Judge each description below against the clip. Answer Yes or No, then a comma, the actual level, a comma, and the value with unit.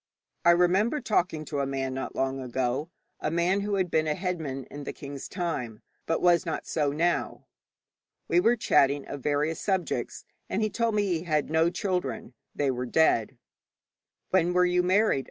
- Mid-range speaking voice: Yes, medium, 160 Hz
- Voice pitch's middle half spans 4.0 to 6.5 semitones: Yes, average, 4.5 semitones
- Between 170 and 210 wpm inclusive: Yes, average, 180 wpm